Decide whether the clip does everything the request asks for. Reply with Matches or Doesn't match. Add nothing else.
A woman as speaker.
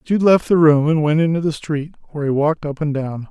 Doesn't match